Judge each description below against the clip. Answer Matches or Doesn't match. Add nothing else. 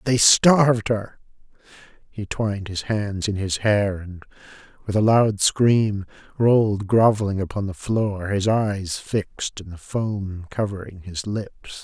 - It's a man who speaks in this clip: Matches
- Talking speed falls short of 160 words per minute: Matches